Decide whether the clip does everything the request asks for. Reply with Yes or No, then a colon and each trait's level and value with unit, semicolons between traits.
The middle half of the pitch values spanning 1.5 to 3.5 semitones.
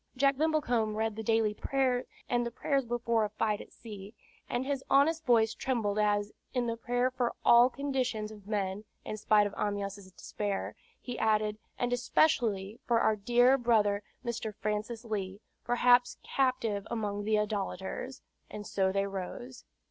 Yes: average, 3.0 semitones